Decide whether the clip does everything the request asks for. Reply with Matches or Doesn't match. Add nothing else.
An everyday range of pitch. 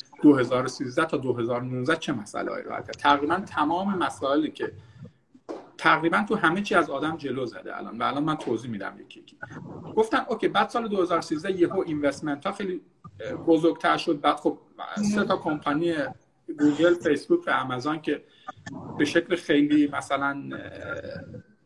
Matches